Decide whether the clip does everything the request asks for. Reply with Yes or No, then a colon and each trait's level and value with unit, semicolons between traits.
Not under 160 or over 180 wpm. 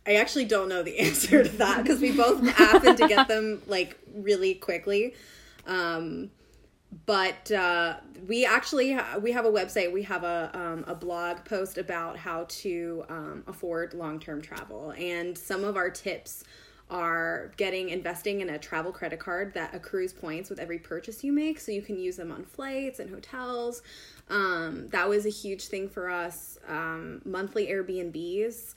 Yes: average, 175 wpm